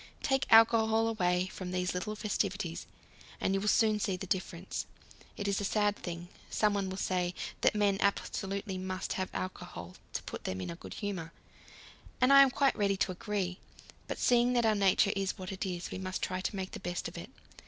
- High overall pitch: Yes, high, 195 Hz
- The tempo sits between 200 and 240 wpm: Yes, fast, 205 wpm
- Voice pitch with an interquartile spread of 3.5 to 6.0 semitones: No, narrow, 2.5 semitones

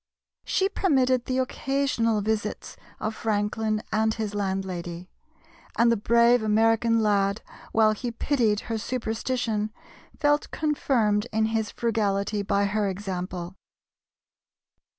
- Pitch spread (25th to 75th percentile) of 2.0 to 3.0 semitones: Yes, narrow, 2.4 semitones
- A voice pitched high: Yes, high, 220 Hz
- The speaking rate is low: Yes, slow, 110 wpm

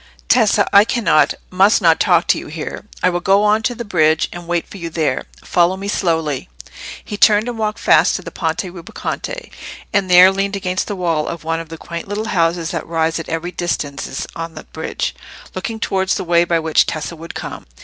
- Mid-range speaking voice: Yes, medium, 175 Hz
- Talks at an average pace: No, fast, 210 wpm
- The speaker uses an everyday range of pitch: Yes, average, 3.4 semitones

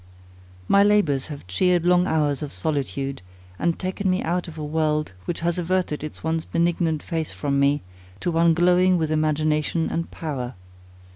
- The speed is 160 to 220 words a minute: Yes, average, 165 wpm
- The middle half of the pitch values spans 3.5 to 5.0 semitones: No, average, 2.7 semitones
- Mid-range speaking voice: Yes, medium, 160 Hz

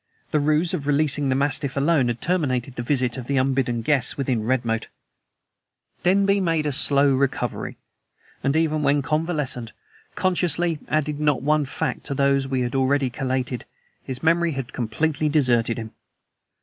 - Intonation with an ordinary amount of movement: Yes, average, 3.0 semitones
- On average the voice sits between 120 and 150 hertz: Yes, medium, 140 Hz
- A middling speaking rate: Yes, average, 160 wpm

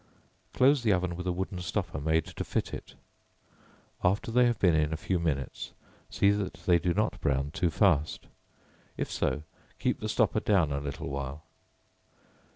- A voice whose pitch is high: No, very low, 90 Hz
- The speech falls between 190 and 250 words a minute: No, average, 170 wpm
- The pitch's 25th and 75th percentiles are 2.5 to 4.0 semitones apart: No, average, 4.5 semitones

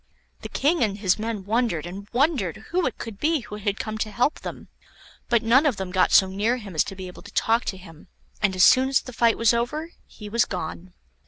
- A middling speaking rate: No, fast, 240 wpm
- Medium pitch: No, high, 215 Hz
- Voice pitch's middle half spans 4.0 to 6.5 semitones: Yes, average, 4.3 semitones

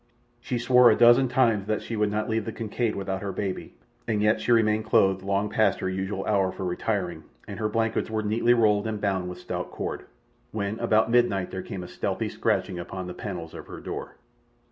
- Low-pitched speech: Yes, low, 105 Hz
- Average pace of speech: No, fast, 210 wpm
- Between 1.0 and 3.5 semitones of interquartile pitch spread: Yes, average, 2.7 semitones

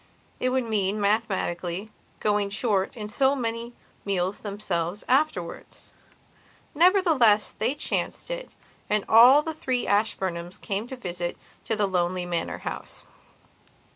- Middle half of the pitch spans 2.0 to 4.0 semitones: No, average, 4.8 semitones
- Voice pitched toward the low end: No, high, 210 Hz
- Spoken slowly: Yes, slow, 130 wpm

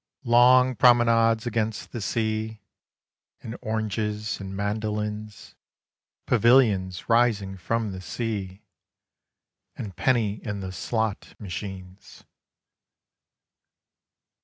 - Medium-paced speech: No, slow, 85 wpm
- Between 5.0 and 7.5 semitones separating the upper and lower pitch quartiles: No, narrow, 2.5 semitones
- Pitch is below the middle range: Yes, low, 110 Hz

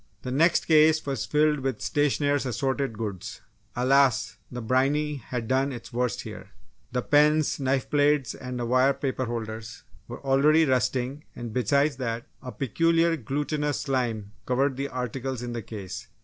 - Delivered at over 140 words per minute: Yes, average, 150 wpm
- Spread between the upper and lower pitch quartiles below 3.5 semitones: Yes, average, 3.0 semitones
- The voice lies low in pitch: Yes, low, 130 Hz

